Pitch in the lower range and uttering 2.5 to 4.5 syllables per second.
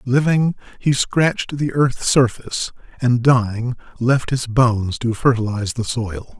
Yes: low, 125 Hz; 4.4 syllables/s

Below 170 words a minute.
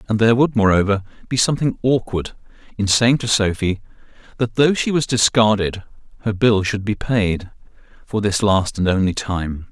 Yes: average, 160 wpm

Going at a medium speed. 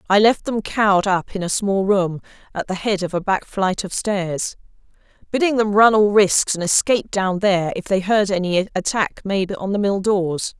No: fast, 210 wpm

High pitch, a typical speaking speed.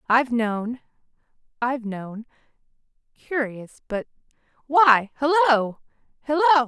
No: very high, 250 Hz; slow, 35 wpm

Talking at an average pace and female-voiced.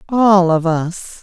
Yes: average, 145 wpm; female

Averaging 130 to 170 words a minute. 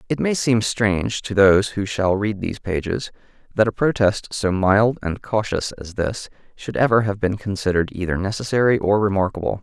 No: average, 180 wpm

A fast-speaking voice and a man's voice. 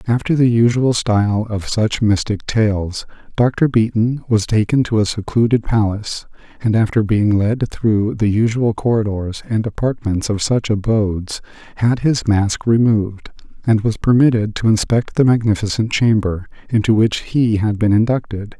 No: average, 150 wpm; male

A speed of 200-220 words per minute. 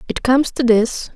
Yes: fast, 205 wpm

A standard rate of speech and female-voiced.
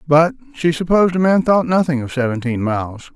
No: average, 190 wpm; male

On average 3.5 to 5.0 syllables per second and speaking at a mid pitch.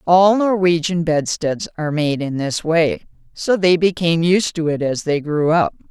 Yes: 4.6 syllables/s; medium, 165 Hz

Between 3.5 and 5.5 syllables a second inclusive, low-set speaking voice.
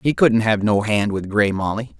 Yes: 4.6 syllables/s; low, 105 Hz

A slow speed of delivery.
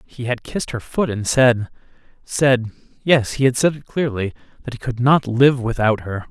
No: average, 200 wpm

